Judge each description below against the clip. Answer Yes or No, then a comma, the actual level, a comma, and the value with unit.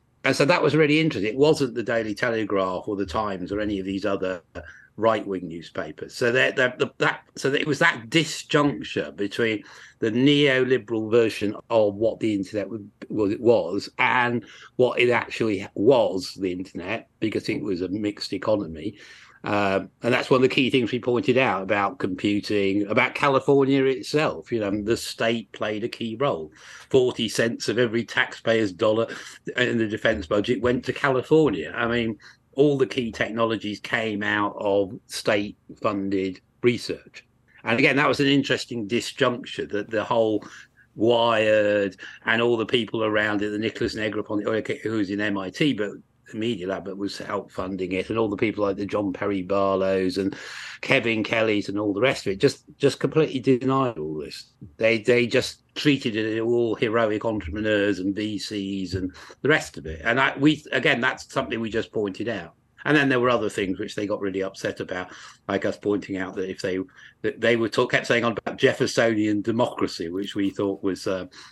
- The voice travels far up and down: No, average, 3.6 semitones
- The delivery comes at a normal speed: Yes, average, 185 wpm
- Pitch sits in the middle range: No, low, 110 Hz